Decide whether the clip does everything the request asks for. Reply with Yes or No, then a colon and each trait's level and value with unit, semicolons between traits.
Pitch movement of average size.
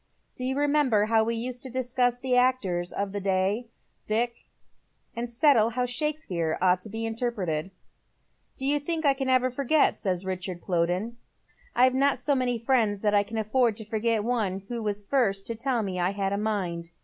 Yes: average, 4.3 semitones